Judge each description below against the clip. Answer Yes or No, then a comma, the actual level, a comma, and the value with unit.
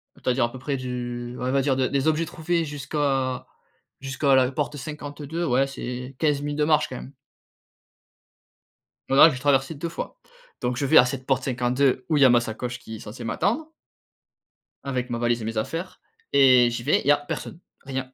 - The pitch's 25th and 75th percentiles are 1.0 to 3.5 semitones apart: Yes, average, 2.8 semitones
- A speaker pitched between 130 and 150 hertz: Yes, low, 135 Hz